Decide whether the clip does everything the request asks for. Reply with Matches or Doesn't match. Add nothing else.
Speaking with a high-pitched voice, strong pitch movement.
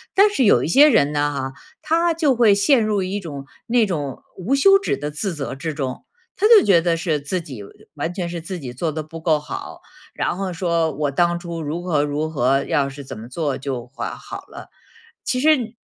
Doesn't match